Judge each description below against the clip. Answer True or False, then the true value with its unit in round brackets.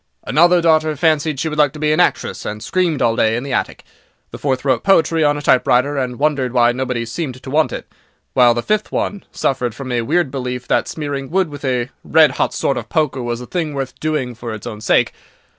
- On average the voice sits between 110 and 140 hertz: True (135 Hz)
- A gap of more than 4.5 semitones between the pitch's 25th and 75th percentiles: False (3.9 semitones)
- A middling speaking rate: False (230 wpm)